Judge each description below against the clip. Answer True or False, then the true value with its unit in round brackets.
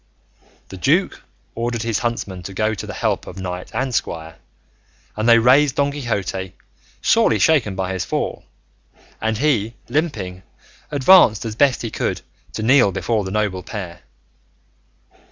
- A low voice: True (110 Hz)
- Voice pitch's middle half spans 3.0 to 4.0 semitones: False (4.7 semitones)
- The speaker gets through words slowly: False (150 wpm)